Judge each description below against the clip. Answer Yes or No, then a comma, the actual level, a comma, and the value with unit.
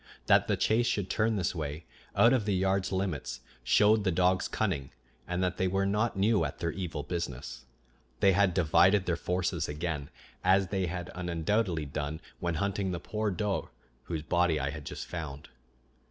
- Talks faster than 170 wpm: Yes, average, 180 wpm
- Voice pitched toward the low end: Yes, very low, 90 Hz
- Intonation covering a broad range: No, average, 3.4 semitones